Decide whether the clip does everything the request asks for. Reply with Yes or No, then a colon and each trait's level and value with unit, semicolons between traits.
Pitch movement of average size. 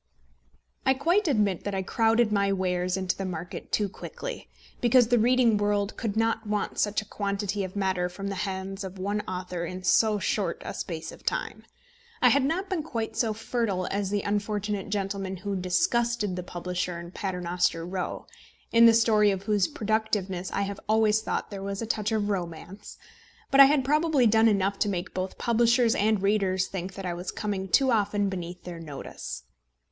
Yes: average, 3.0 semitones